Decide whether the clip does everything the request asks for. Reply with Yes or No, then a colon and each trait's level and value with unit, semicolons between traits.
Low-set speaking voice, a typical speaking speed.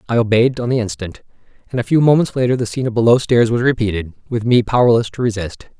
No: low, 120 Hz; fast, 230 wpm